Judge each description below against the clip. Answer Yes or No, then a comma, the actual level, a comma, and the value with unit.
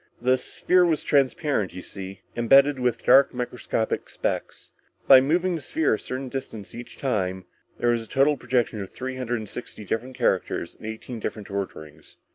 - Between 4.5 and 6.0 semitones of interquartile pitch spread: No, average, 4.0 semitones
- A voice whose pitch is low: Yes, low, 125 Hz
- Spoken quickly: No, average, 175 wpm